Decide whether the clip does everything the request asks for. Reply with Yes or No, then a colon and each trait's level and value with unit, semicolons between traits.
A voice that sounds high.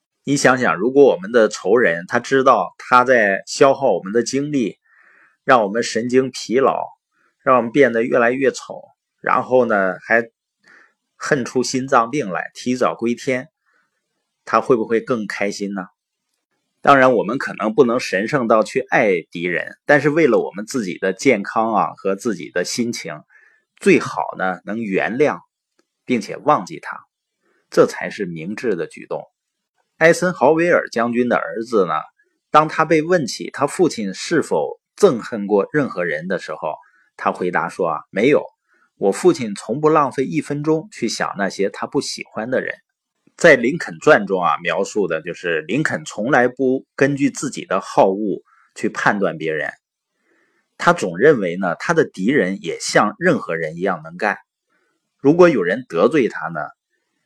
No: low, 135 Hz